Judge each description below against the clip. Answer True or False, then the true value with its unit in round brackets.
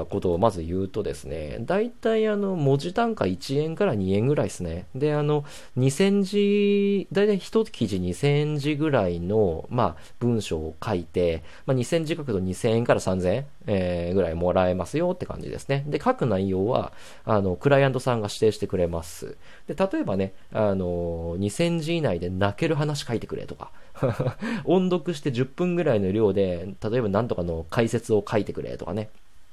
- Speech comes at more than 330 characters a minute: False (310 characters per minute)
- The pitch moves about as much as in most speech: False (8.8 semitones)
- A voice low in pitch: True (115 Hz)